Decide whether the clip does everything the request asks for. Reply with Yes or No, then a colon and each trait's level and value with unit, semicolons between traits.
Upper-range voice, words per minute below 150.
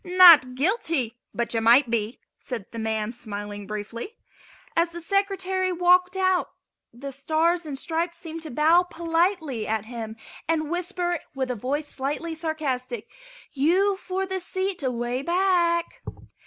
Yes: very high, 315 Hz; average, 140 wpm